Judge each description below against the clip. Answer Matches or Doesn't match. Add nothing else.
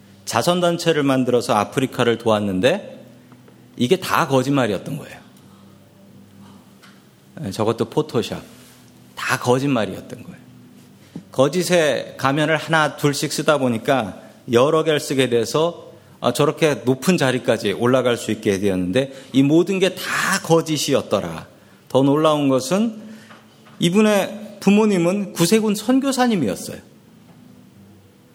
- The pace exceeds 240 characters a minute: Matches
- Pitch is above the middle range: Doesn't match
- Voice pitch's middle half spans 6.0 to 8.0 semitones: Matches